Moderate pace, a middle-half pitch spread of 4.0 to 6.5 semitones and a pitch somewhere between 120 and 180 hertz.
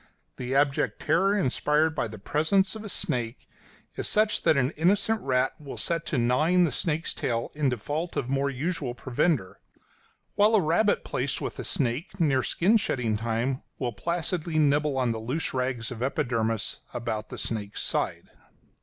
Yes: average, 165 wpm; wide, 5.5 semitones; medium, 140 Hz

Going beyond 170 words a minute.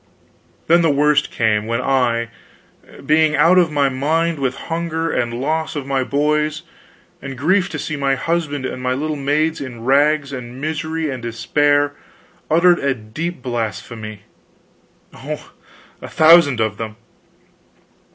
No: average, 140 wpm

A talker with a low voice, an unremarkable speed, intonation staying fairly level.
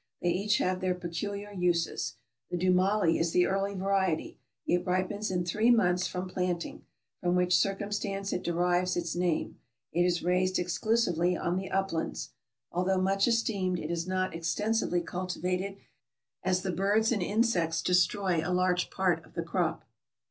No: medium, 185 Hz; average, 160 wpm; narrow, 1.9 semitones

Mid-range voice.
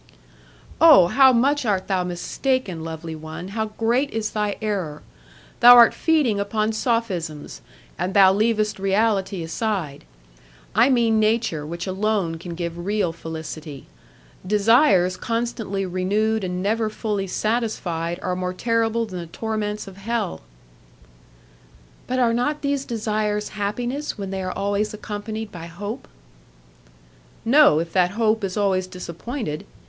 No: high, 205 Hz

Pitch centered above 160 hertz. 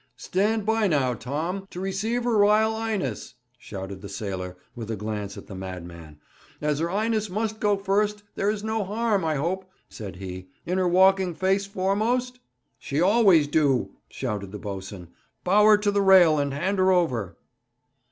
Yes: medium, 185 Hz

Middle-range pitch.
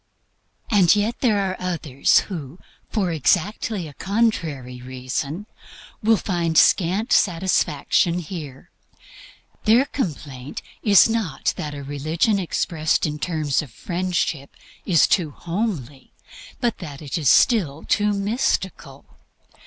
Yes: medium, 170 Hz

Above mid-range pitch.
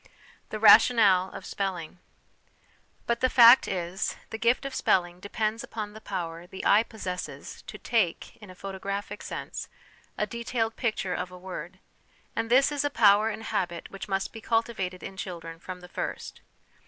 Yes: high, 200 Hz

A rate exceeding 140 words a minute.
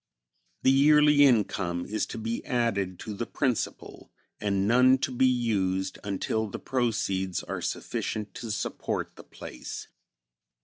No: slow, 135 wpm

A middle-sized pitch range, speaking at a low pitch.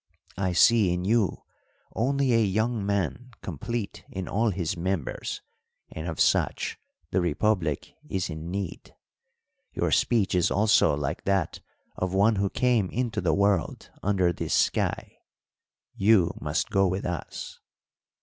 Yes: average, 3.7 semitones; very low, 95 Hz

